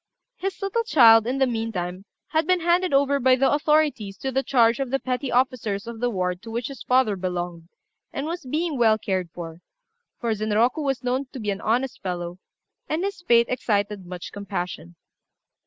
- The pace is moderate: Yes, average, 190 wpm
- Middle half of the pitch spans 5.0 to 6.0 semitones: Yes, wide, 5.5 semitones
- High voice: Yes, high, 240 Hz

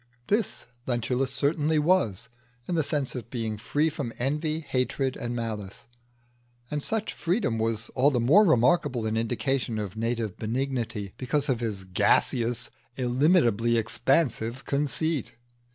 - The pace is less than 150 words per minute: Yes, slow, 135 wpm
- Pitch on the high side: No, low, 125 Hz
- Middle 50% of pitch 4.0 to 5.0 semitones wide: Yes, average, 4.4 semitones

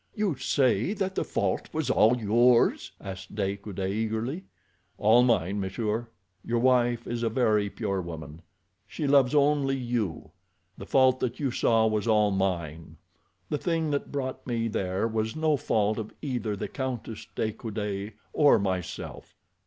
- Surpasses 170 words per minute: No, average, 155 wpm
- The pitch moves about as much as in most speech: Yes, average, 4.4 semitones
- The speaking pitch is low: Yes, low, 115 Hz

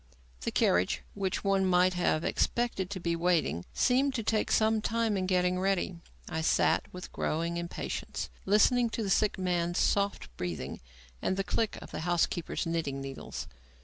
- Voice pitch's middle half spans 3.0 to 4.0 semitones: Yes, average, 3.4 semitones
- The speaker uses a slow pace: No, average, 165 wpm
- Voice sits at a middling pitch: Yes, medium, 180 Hz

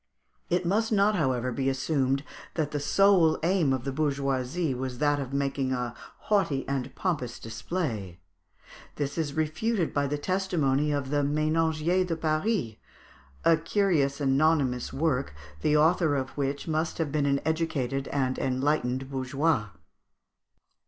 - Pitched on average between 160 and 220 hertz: No, medium, 145 Hz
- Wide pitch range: No, average, 3.4 semitones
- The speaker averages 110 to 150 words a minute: Yes, average, 140 wpm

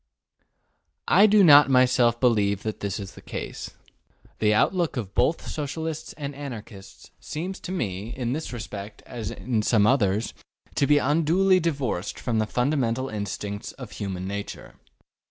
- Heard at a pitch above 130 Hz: No, low, 125 Hz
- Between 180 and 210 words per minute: No, average, 150 wpm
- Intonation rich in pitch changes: Yes, wide, 6.0 semitones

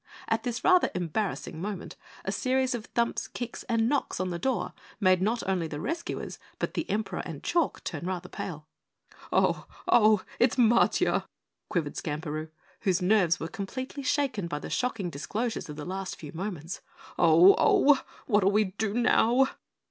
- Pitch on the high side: Yes, high, 200 Hz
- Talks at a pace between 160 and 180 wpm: Yes, average, 165 wpm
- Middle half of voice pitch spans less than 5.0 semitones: No, wide, 5.6 semitones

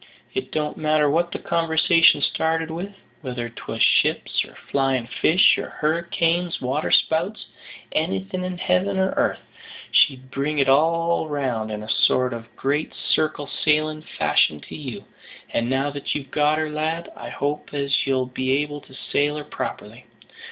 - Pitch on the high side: No, medium, 150 Hz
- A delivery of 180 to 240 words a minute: No, average, 160 wpm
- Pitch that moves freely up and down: No, average, 3.6 semitones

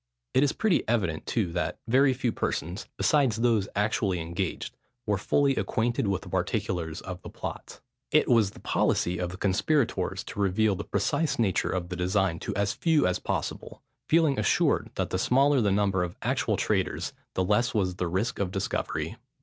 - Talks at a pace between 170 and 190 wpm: Yes, average, 180 wpm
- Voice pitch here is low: Yes, low, 100 Hz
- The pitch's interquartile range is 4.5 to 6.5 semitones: Yes, average, 4.8 semitones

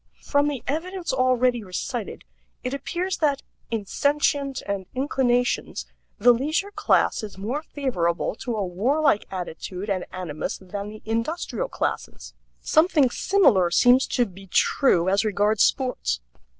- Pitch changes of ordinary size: No, wide, 6.3 semitones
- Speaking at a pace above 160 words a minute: No, slow, 135 wpm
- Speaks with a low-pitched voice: No, high, 245 Hz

